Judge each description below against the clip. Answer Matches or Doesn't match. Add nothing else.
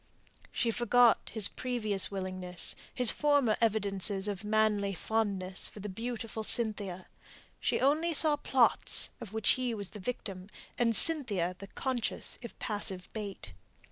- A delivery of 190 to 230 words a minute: Doesn't match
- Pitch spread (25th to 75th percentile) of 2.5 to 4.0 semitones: Matches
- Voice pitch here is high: Matches